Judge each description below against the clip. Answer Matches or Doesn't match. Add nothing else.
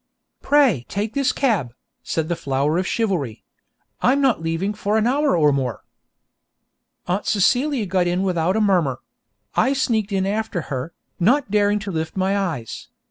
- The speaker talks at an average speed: Matches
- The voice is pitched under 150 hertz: Doesn't match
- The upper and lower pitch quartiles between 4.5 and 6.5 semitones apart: Matches